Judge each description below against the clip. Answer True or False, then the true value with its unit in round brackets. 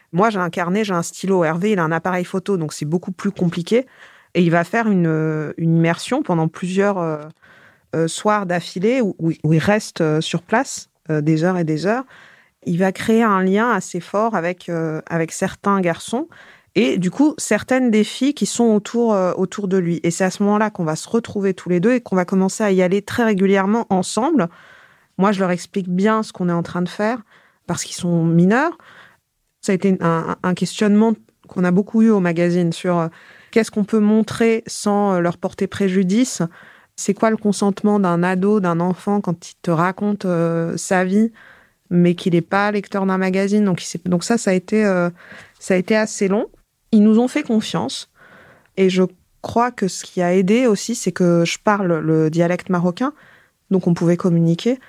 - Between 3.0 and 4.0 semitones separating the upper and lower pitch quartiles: True (3.6 semitones)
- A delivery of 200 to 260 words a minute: True (205 wpm)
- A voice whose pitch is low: False (190 Hz)